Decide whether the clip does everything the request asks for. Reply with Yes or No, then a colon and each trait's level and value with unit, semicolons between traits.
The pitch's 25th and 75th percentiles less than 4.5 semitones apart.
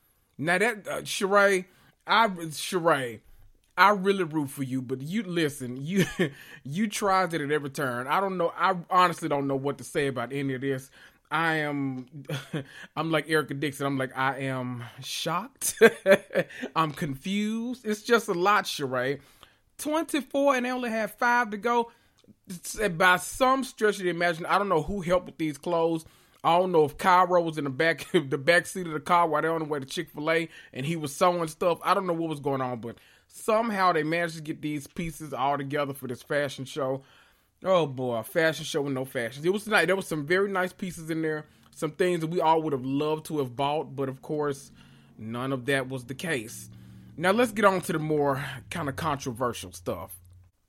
No: average, 5.0 semitones